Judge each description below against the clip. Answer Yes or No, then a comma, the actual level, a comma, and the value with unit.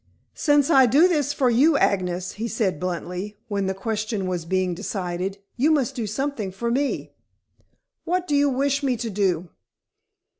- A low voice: No, high, 220 Hz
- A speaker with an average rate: Yes, average, 165 wpm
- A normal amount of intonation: No, wide, 6.7 semitones